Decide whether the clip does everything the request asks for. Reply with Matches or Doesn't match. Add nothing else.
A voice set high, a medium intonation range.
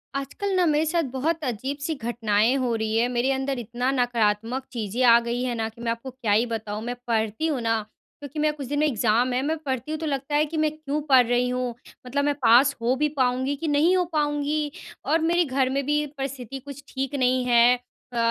Matches